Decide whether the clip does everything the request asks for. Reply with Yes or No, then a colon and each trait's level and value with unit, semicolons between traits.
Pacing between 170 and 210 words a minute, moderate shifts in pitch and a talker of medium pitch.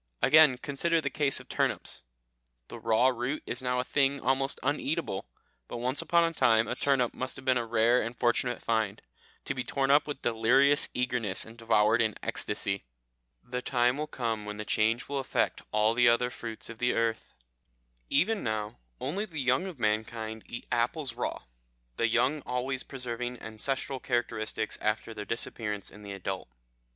No: average, 175 wpm; average, 3.2 semitones; low, 125 Hz